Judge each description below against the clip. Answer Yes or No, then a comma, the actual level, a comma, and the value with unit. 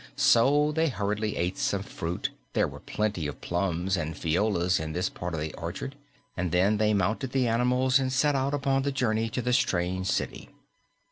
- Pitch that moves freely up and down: Yes, wide, 6.6 semitones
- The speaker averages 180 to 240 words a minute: Yes, average, 190 wpm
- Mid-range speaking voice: No, low, 105 Hz